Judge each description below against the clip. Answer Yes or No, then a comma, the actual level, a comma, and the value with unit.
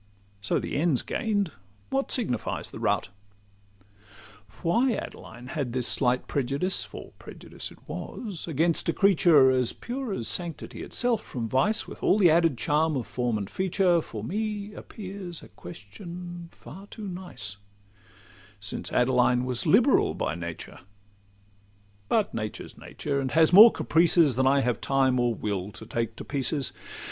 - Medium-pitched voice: Yes, medium, 150 Hz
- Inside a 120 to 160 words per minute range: Yes, average, 155 wpm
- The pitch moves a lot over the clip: Yes, wide, 7.3 semitones